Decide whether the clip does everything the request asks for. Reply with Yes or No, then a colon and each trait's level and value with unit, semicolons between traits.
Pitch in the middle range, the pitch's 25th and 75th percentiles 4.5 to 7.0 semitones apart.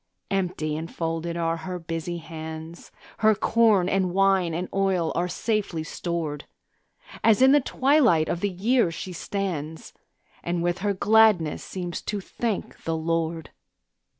No: medium, 175 Hz; average, 3.3 semitones